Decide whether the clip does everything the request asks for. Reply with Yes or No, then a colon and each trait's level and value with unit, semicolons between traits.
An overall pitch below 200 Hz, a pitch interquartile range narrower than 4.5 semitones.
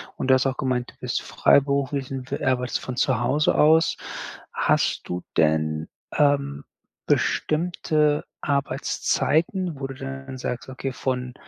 Yes: low, 135 Hz; narrow, 2.4 semitones